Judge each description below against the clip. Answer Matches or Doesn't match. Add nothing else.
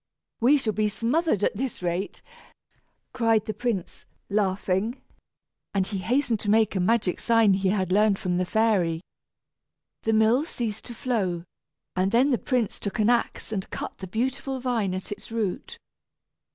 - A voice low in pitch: Doesn't match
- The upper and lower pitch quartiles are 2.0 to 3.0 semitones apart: Doesn't match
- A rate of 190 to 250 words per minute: Doesn't match